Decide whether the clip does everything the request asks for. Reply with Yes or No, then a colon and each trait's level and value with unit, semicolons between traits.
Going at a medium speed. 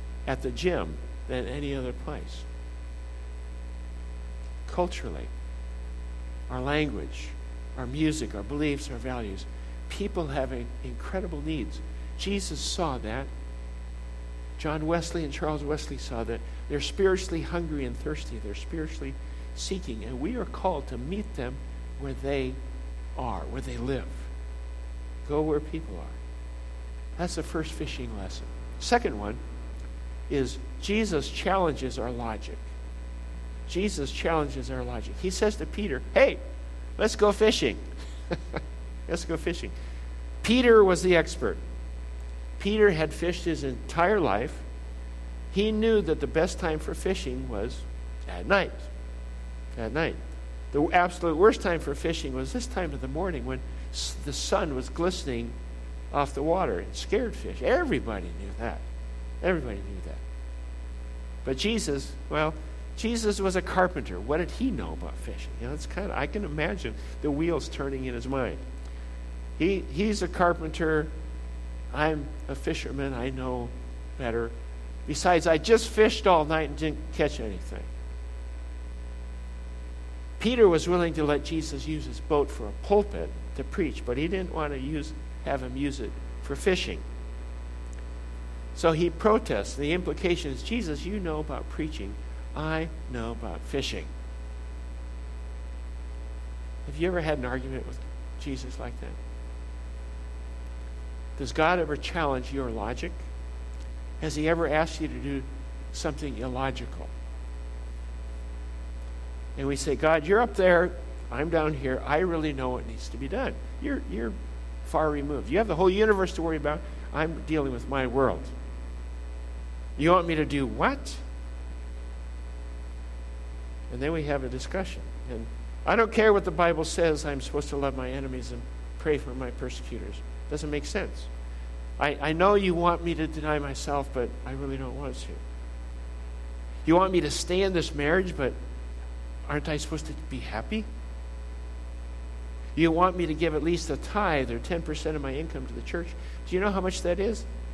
Yes: average, 150 wpm